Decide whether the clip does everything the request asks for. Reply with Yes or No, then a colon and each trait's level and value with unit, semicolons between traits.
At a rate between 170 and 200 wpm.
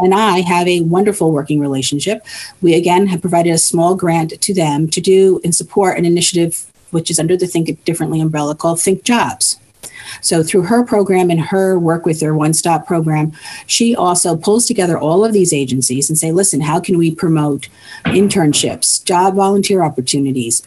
Yes: average, 180 wpm